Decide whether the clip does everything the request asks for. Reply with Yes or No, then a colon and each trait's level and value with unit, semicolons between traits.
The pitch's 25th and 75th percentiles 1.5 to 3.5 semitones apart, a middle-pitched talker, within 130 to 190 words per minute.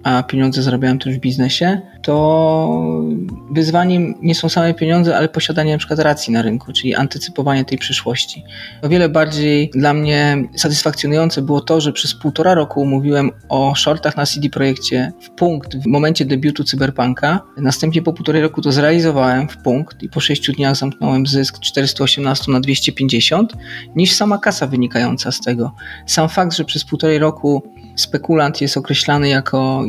Yes: average, 2.9 semitones; medium, 145 Hz; fast, 160 wpm